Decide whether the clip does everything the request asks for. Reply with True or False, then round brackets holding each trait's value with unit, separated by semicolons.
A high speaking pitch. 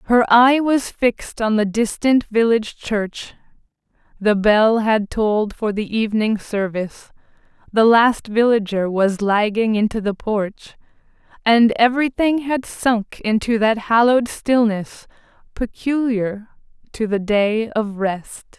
True (220 Hz)